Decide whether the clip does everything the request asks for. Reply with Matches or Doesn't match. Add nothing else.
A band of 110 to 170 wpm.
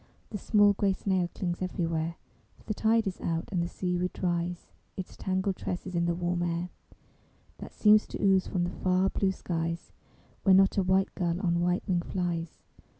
Doesn't match